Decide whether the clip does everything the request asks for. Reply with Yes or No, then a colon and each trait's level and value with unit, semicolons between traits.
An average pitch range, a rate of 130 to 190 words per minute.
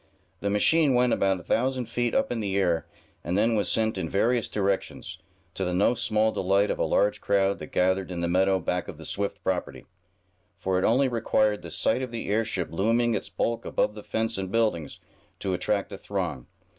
No: average, 3.3 semitones; fast, 205 wpm